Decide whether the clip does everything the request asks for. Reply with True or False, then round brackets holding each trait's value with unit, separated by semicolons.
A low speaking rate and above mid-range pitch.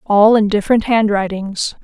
True (130 wpm; 210 Hz)